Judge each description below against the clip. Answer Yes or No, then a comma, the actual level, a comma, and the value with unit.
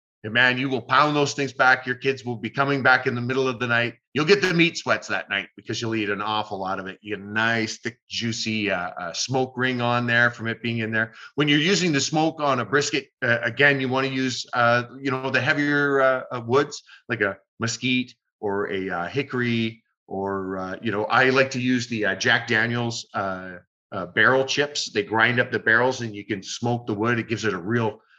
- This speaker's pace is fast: Yes, fast, 240 wpm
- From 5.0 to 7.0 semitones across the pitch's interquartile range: No, average, 3.0 semitones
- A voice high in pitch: No, low, 120 Hz